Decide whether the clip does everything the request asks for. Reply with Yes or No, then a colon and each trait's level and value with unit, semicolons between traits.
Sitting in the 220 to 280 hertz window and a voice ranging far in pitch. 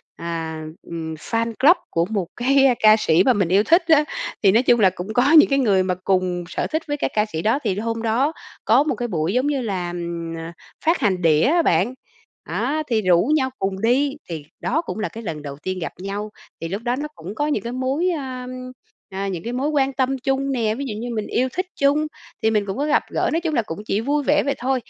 Yes: high, 225 Hz; wide, 6.6 semitones